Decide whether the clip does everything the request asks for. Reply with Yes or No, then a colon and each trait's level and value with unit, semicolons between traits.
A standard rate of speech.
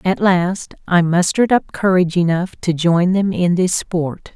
Yes: average, 180 wpm